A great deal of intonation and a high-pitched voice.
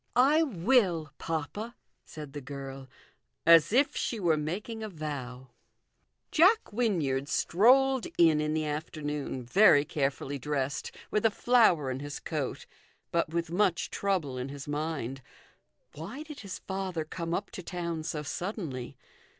No: wide, 6.0 semitones; medium, 160 Hz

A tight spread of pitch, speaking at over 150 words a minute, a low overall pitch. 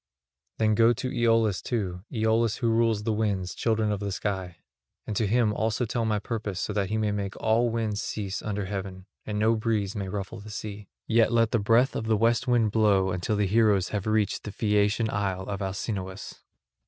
Yes: narrow, 2.1 semitones; fast, 205 wpm; low, 105 Hz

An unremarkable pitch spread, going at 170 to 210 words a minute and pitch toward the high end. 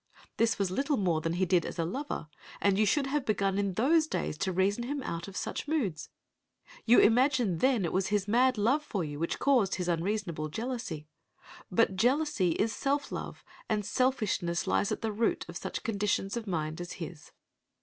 No: wide, 6.1 semitones; average, 195 wpm; high, 205 Hz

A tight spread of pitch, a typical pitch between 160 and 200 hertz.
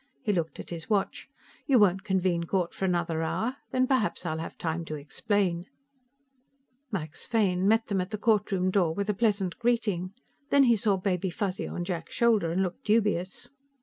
No: average, 3.5 semitones; high, 190 Hz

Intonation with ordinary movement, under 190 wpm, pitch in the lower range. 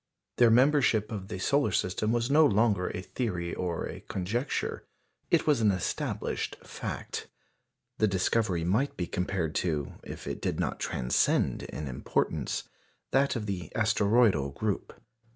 Yes: average, 4.7 semitones; average, 145 wpm; low, 105 Hz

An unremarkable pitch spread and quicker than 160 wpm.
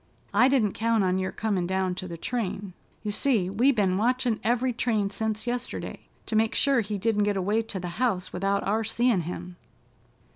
Yes: average, 3.7 semitones; average, 190 wpm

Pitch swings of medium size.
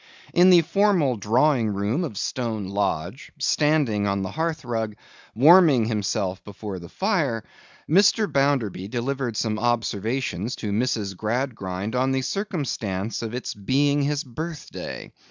No: wide, 5.8 semitones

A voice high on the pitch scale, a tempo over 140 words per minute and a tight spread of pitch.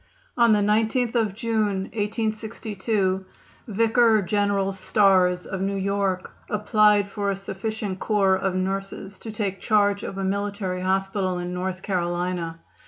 No: high, 200 Hz; slow, 135 wpm; narrow, 2.0 semitones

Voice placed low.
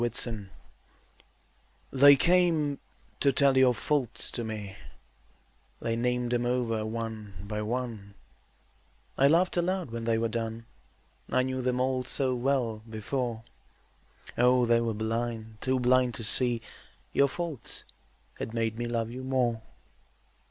Yes: low, 120 Hz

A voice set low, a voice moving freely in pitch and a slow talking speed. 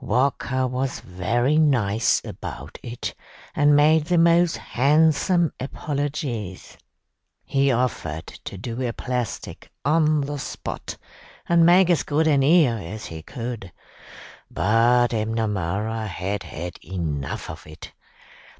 Yes: low, 125 Hz; wide, 5.9 semitones; slow, 120 wpm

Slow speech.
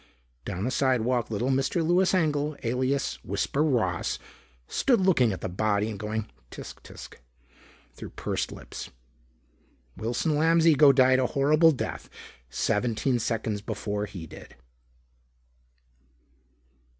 Yes: slow, 120 wpm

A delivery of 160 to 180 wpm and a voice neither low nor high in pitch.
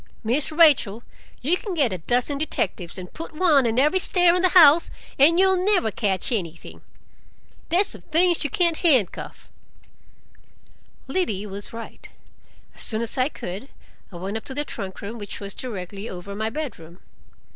No: average, 165 wpm; very high, 255 Hz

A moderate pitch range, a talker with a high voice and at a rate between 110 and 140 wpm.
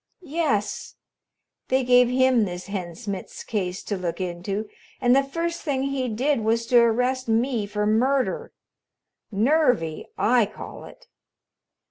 Yes: average, 4.5 semitones; high, 235 Hz; slow, 135 wpm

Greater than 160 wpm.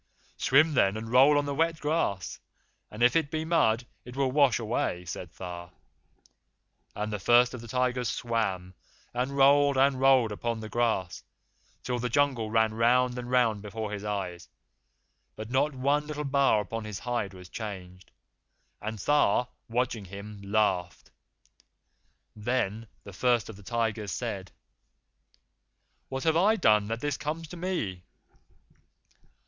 No: average, 155 wpm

